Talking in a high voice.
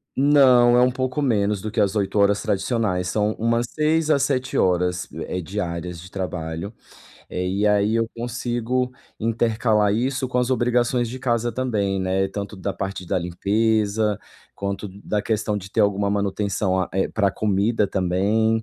No: low, 105 Hz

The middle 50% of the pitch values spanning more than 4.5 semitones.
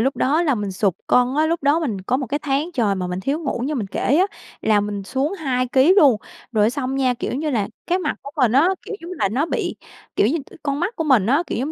Yes: average, 5.3 semitones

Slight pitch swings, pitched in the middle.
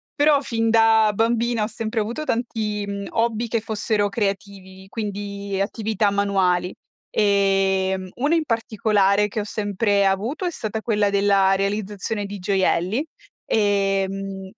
No: narrow, 2.3 semitones; high, 205 Hz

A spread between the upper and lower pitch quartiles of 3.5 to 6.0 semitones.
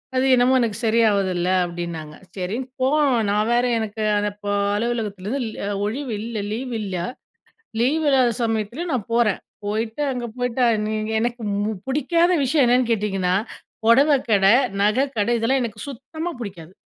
Yes: average, 3.8 semitones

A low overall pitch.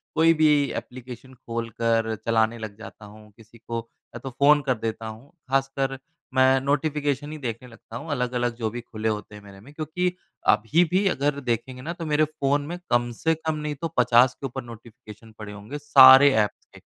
Yes: low, 125 Hz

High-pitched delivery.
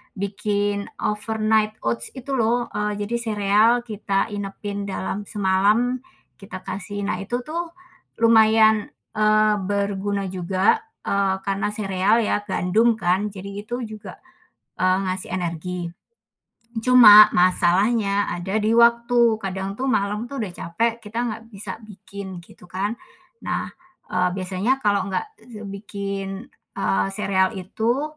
Yes: high, 205 Hz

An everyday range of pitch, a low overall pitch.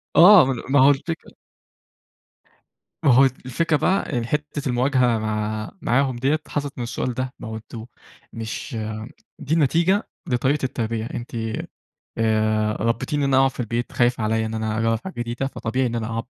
Yes: average, 3.5 semitones; low, 125 Hz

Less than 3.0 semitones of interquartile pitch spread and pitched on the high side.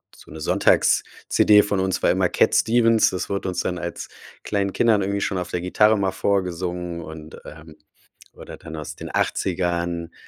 No: narrow, 2.6 semitones; very low, 90 Hz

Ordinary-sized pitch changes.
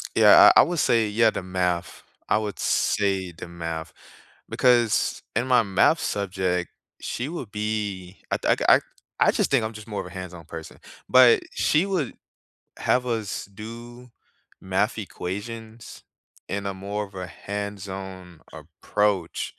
Yes: average, 3.6 semitones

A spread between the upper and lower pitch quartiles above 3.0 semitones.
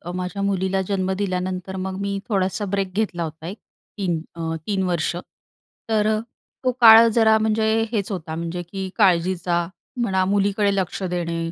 No: narrow, 2.4 semitones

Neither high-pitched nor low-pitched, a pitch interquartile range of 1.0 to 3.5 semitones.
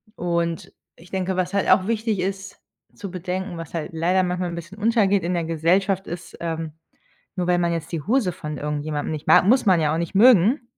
Yes: medium, 180 Hz; average, 2.8 semitones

